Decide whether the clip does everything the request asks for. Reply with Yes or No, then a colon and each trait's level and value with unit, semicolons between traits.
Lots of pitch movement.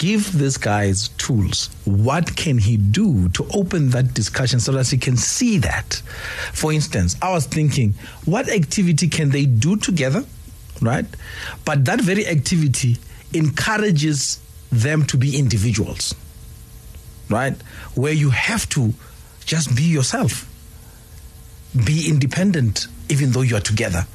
Yes: wide, 6.5 semitones